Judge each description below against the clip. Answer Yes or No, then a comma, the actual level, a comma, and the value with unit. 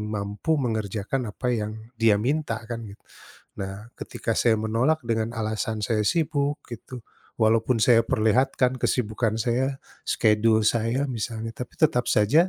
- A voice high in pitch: No, low, 115 Hz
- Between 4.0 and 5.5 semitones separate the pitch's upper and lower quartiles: No, average, 2.7 semitones